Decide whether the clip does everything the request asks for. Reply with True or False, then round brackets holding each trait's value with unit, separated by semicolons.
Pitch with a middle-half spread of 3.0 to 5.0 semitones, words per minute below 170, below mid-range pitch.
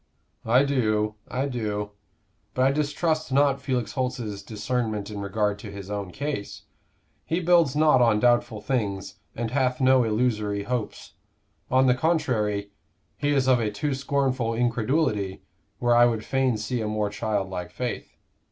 True (4.1 semitones; 150 wpm; 120 Hz)